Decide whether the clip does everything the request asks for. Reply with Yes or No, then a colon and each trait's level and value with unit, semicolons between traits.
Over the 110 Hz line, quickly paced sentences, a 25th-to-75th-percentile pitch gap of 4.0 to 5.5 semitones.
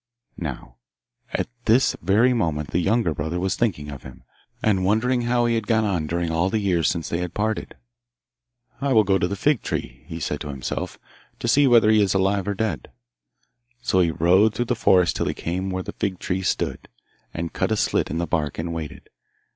No: very low, 95 Hz; fast, 210 wpm; average, 4.9 semitones